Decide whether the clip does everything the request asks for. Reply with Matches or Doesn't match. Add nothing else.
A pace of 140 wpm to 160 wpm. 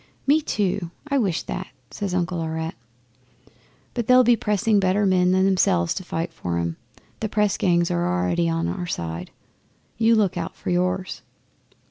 Doesn't match